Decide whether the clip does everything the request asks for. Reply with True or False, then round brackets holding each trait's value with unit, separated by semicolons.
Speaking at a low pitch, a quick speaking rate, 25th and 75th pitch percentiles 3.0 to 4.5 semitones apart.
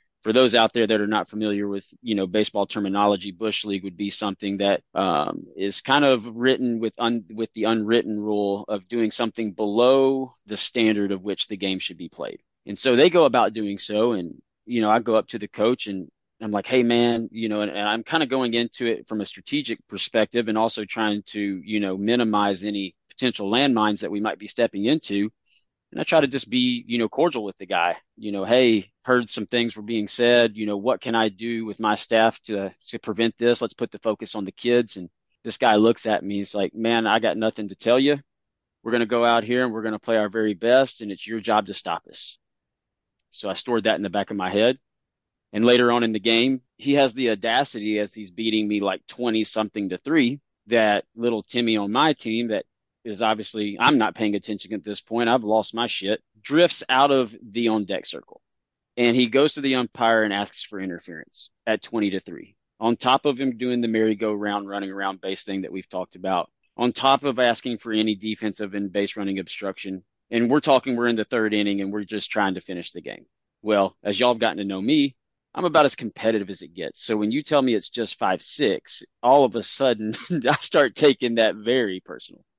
False (110 Hz; 230 wpm; 2.6 semitones)